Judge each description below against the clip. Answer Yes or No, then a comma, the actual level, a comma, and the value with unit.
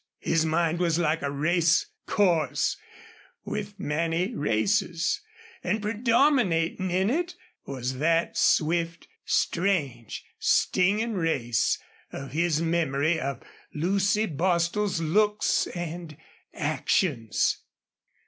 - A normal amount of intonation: Yes, average, 4.0 semitones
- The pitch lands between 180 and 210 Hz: No, medium, 170 Hz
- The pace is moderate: No, slow, 90 wpm